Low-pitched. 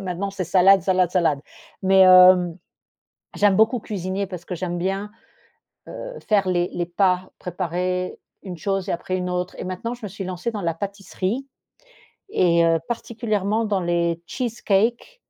No: medium, 185 Hz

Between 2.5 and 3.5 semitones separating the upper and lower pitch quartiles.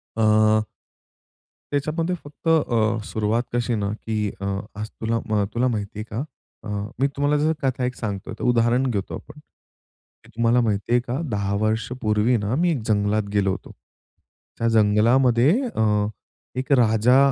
Yes: average, 3.0 semitones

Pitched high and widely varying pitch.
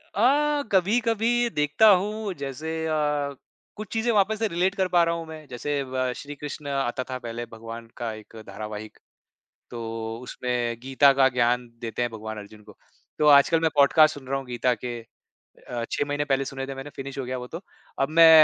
No: low, 135 Hz; wide, 5.7 semitones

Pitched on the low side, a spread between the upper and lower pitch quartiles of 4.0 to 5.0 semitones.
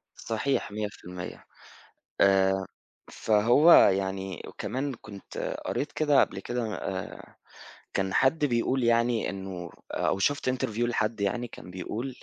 Yes: low, 110 Hz; average, 4.5 semitones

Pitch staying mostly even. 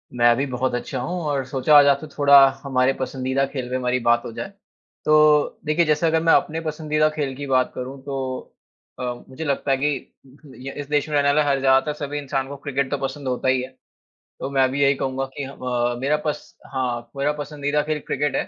Yes: narrow, 2.2 semitones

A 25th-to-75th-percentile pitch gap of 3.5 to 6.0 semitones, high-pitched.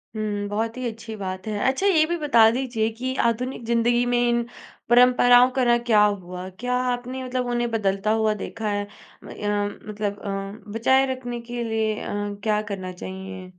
No: average, 2.9 semitones; high, 225 Hz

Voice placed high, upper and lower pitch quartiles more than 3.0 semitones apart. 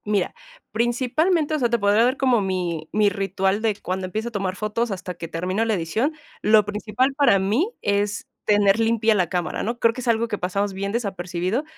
Yes: high, 210 Hz; average, 3.5 semitones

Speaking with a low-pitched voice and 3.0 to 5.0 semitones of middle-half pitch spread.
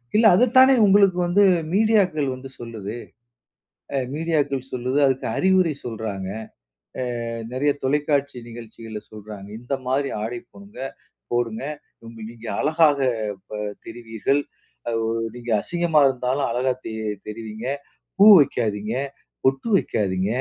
No: low, 130 Hz; wide, 5.5 semitones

